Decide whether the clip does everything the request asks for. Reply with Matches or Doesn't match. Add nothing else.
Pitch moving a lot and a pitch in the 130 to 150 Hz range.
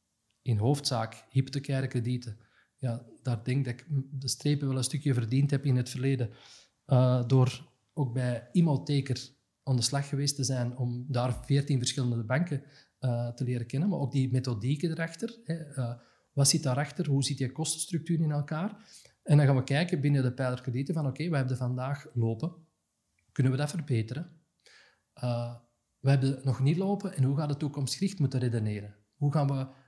Doesn't match